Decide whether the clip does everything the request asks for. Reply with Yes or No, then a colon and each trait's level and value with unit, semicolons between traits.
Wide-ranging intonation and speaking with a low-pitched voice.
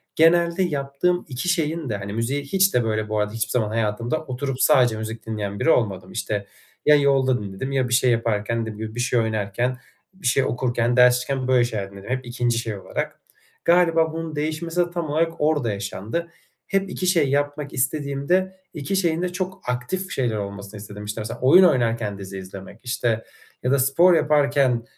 Yes: wide, 6.0 semitones; low, 125 Hz